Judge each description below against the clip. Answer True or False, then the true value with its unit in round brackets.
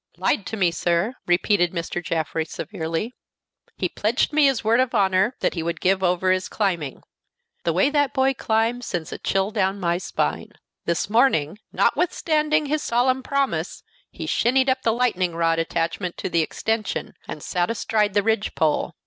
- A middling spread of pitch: False (6.2 semitones)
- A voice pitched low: False (200 Hz)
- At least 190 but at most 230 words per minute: False (175 wpm)